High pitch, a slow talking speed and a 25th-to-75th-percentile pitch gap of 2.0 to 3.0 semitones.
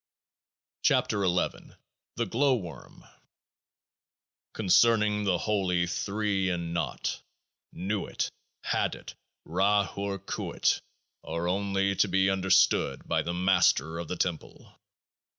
No: very low, 95 Hz; slow, 110 wpm; narrow, 2.6 semitones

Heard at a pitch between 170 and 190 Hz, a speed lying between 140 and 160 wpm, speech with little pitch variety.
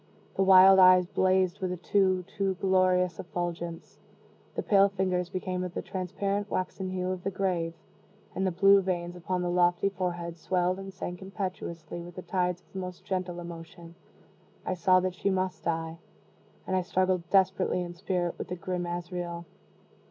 No: medium, 185 Hz; average, 175 wpm; narrow, 1.3 semitones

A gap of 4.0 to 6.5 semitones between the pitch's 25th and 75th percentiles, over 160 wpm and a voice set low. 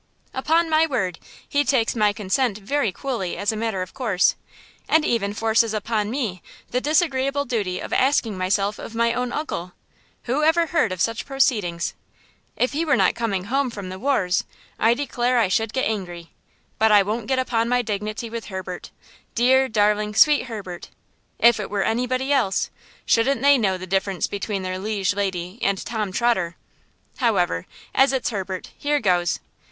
No: average, 4.9 semitones; average, 170 wpm; high, 225 Hz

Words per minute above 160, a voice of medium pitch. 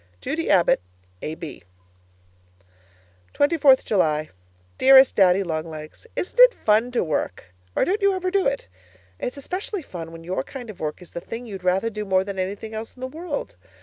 No: average, 180 wpm; high, 215 Hz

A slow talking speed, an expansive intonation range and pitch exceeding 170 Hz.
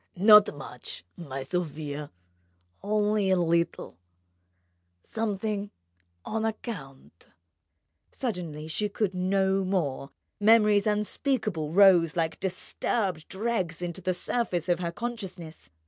No: slow, 105 wpm; average, 4.4 semitones; medium, 185 Hz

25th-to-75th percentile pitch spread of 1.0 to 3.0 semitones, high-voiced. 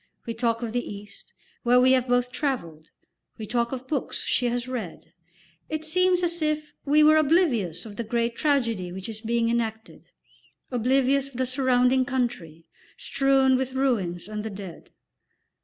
No: average, 3.5 semitones; high, 245 Hz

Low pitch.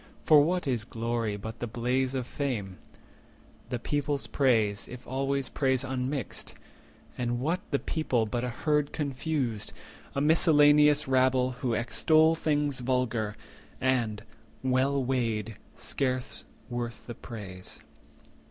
Yes: low, 130 Hz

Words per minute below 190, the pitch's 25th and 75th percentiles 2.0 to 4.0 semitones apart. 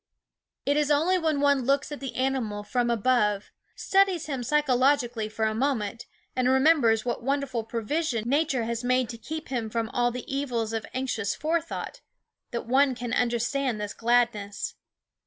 Yes: average, 160 wpm; average, 3.6 semitones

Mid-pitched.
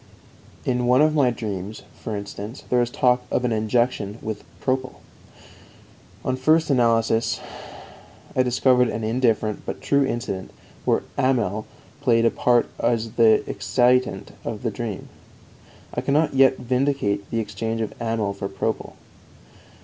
No: low, 120 Hz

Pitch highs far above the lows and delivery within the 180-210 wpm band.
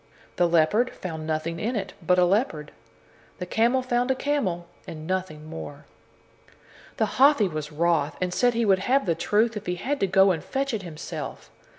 Yes: wide, 6.3 semitones; average, 190 wpm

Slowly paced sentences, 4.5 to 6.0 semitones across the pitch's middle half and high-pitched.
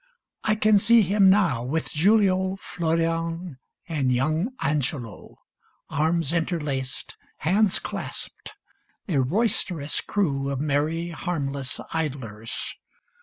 No: slow, 100 wpm; average, 5.1 semitones; medium, 160 Hz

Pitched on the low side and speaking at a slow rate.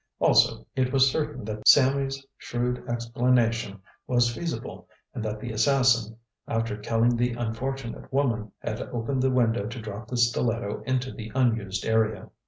No: low, 120 Hz; average, 150 wpm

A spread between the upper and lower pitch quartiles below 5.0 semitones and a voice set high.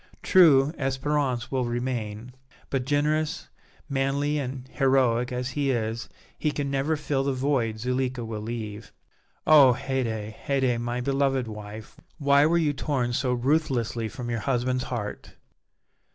No: average, 2.8 semitones; low, 130 Hz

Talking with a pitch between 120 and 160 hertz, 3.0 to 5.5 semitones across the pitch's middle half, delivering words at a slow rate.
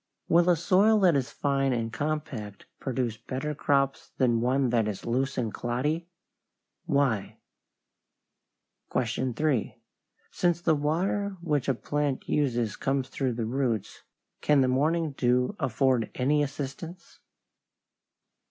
Yes: low, 135 Hz; average, 3.6 semitones; slow, 125 wpm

